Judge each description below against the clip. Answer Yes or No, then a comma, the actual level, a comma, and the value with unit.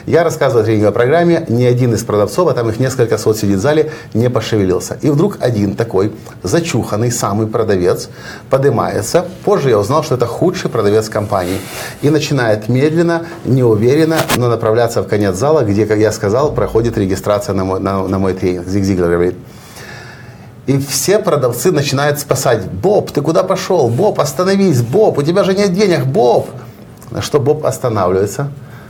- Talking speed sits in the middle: No, fast, 165 wpm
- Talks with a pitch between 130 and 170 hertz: No, low, 120 Hz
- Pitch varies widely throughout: Yes, wide, 5.9 semitones